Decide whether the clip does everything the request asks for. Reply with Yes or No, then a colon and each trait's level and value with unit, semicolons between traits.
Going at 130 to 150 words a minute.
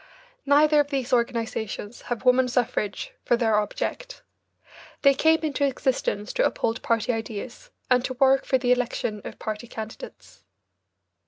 Yes: average, 145 wpm